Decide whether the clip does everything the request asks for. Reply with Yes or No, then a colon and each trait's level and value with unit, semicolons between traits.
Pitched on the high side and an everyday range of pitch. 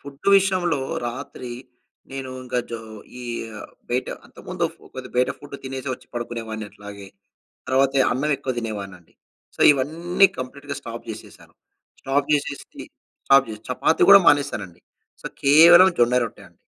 No: low, 130 Hz; average, 3.5 semitones